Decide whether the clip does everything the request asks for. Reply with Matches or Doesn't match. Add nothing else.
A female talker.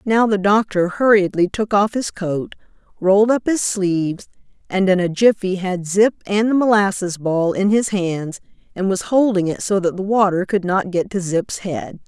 Matches